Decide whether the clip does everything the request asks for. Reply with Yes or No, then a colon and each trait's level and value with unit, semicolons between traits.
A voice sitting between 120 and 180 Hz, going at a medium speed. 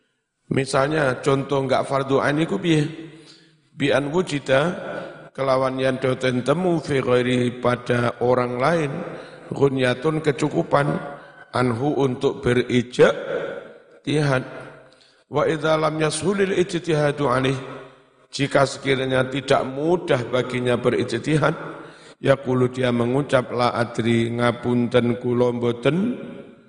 Yes: low, 135 Hz; average, 95 wpm